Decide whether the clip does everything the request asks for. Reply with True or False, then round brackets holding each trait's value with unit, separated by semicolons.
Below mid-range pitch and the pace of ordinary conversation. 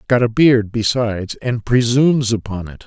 True (115 Hz; 170 wpm)